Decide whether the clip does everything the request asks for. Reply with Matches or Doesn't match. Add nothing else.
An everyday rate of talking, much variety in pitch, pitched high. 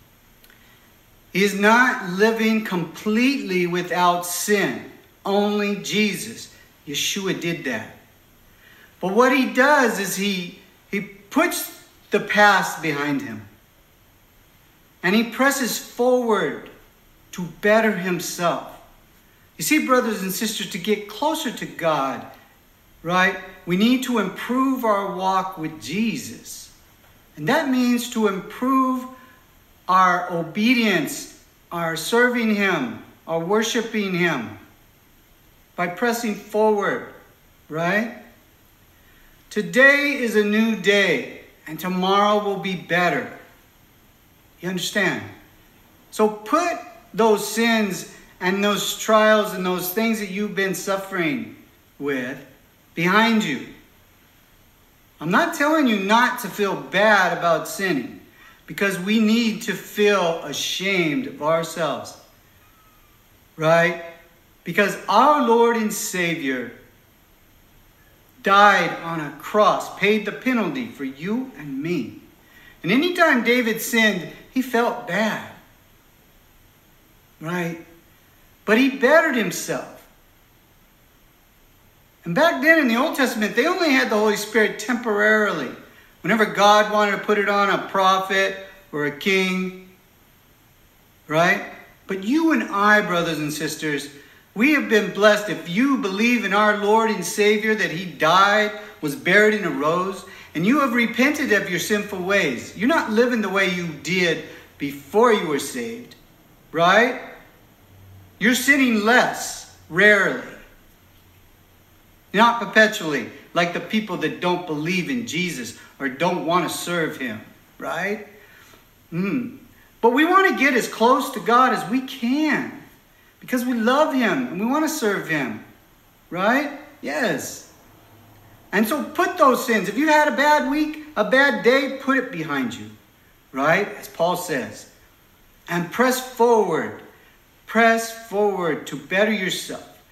Doesn't match